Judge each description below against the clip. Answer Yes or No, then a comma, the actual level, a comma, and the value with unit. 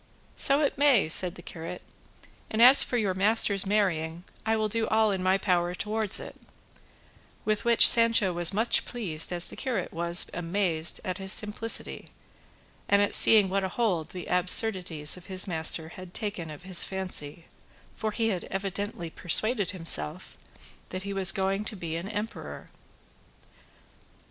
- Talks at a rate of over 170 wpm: No, average, 165 wpm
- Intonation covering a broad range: No, average, 3.7 semitones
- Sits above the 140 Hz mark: Yes, high, 190 Hz